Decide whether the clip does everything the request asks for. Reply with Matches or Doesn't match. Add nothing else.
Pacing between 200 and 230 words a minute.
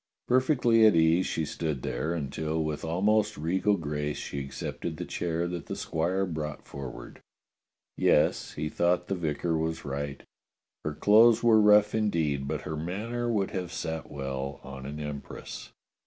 Doesn't match